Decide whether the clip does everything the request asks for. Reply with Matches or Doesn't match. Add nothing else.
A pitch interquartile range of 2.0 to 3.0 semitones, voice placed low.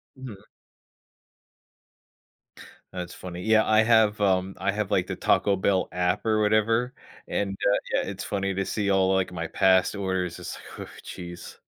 Matches